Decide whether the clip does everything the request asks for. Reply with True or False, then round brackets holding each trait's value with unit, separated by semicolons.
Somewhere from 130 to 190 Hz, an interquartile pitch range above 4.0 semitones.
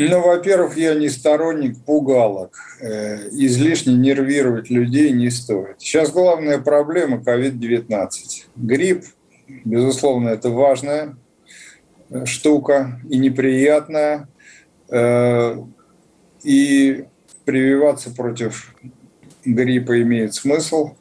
False (135 Hz; 3.7 semitones)